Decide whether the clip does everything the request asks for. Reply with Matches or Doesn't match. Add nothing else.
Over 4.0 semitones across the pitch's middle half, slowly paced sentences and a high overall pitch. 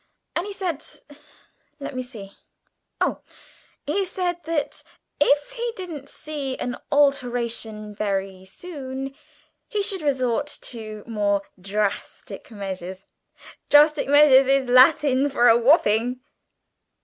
Matches